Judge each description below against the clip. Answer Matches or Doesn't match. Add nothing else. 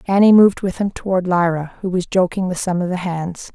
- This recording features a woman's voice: Matches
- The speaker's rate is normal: Doesn't match